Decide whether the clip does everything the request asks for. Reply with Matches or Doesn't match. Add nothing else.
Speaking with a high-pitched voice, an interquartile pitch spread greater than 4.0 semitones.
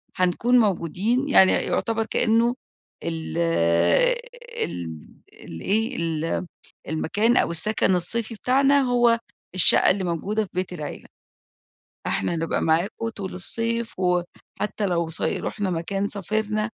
Matches